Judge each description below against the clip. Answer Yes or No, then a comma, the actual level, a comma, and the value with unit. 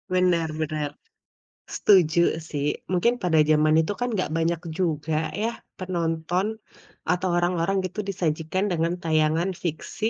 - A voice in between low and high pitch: Yes, medium, 170 Hz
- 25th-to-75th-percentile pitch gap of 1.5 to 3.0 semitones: Yes, narrow, 2.6 semitones